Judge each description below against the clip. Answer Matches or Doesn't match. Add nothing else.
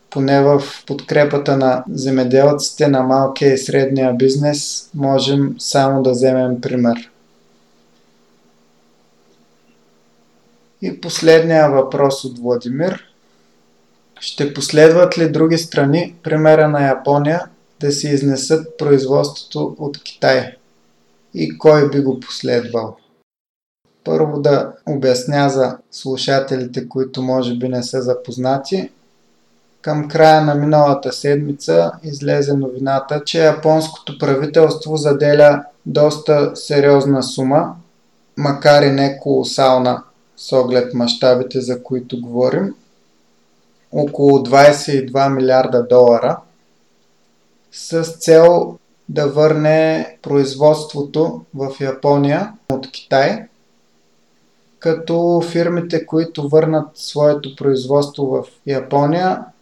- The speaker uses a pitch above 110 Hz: Matches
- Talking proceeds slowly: Matches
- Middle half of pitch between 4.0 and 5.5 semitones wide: Doesn't match